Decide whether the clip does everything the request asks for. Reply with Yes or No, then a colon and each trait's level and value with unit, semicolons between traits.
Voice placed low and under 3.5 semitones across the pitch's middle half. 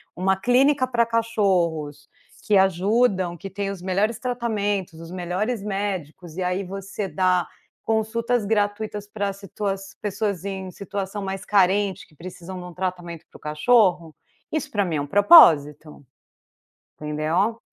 No: high, 195 Hz; average, 3.0 semitones